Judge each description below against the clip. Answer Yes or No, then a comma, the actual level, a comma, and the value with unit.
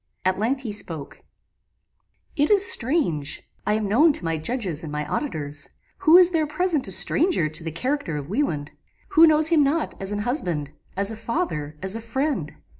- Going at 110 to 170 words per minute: No, average, 190 wpm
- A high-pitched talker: Yes, high, 220 Hz